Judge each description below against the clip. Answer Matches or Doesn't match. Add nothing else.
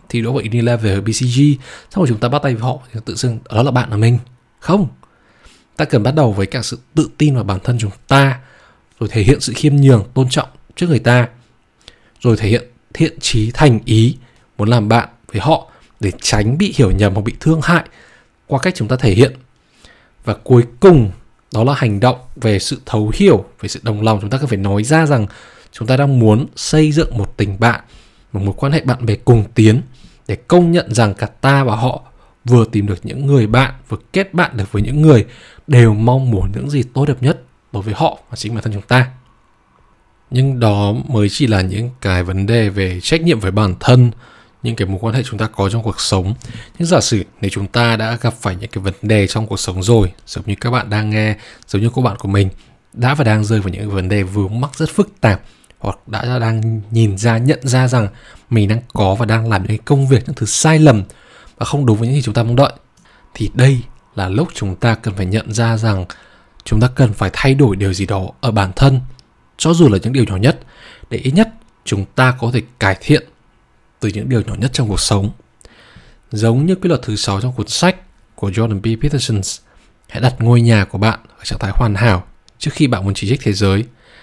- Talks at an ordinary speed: Matches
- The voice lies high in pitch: Doesn't match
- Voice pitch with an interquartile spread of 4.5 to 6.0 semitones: Doesn't match